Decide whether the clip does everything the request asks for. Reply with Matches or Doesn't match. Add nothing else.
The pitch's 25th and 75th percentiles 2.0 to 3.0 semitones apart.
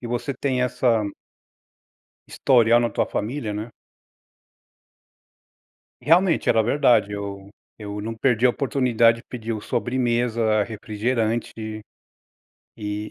Matches